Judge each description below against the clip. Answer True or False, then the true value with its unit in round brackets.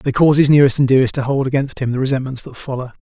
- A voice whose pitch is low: True (130 Hz)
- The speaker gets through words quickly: True (275 wpm)